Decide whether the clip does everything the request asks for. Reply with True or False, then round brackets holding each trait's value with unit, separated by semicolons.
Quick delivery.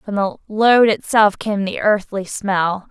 False (165 wpm)